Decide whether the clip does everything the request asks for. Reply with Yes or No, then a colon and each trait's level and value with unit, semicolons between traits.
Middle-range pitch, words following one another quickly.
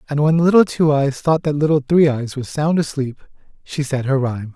Yes: medium, 145 Hz; fast, 225 wpm